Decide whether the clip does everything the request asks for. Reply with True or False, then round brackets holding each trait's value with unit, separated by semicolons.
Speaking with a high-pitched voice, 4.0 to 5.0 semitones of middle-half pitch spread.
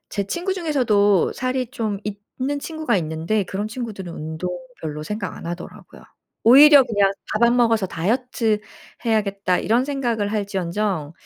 True (210 Hz; 4.6 semitones)